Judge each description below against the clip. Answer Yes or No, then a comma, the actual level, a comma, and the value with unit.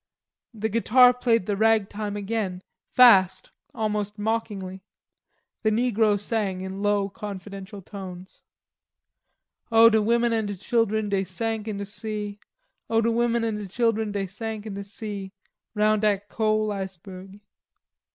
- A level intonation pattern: Yes, narrow, 2.2 semitones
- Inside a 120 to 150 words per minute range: Yes, average, 140 wpm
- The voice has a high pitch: Yes, high, 210 Hz